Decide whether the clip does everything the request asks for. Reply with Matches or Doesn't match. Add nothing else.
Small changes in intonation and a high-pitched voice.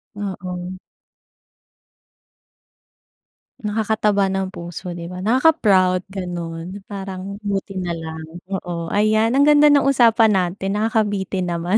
Doesn't match